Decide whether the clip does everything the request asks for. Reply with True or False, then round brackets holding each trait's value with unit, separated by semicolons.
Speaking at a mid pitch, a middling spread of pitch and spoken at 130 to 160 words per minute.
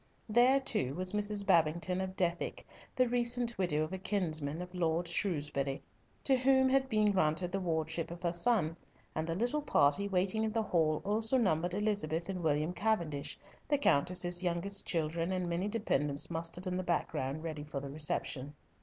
False (180 Hz; 4.7 semitones; 175 wpm)